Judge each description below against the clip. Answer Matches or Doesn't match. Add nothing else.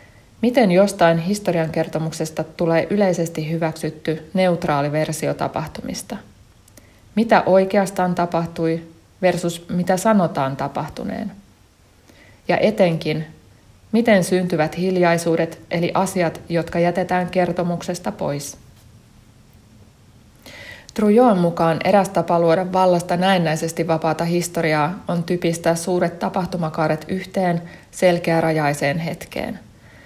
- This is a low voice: Doesn't match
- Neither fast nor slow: Doesn't match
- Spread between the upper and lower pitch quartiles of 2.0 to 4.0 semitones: Matches